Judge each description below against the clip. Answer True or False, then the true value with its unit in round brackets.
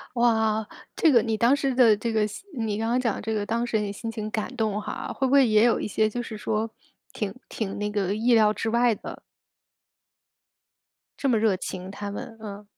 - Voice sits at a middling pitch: False (220 Hz)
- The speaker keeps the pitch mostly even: True (2.0 semitones)